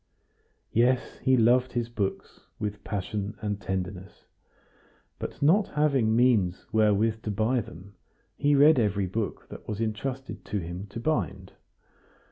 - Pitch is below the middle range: Yes, low, 110 Hz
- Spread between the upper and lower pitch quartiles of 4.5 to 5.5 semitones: No, average, 4.1 semitones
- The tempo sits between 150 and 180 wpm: No, slow, 135 wpm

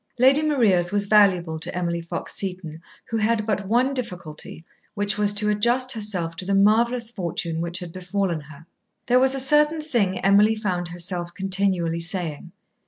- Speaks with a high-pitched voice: Yes, high, 195 Hz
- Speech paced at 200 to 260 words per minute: No, average, 170 wpm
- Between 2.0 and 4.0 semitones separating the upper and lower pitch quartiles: No, average, 4.5 semitones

